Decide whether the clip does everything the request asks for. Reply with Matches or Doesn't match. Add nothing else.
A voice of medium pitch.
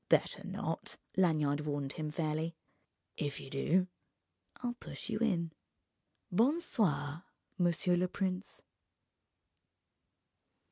Matches